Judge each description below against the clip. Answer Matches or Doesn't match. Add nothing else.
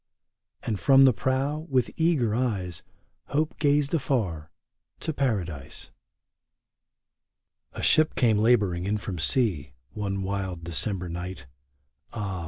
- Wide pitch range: Matches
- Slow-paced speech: Matches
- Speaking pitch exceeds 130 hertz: Doesn't match